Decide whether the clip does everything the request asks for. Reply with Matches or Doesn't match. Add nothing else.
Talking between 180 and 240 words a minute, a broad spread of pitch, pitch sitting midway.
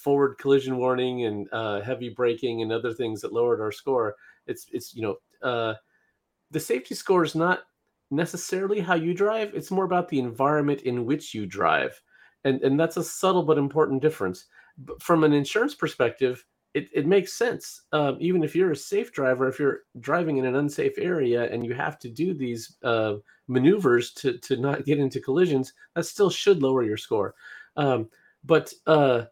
Matches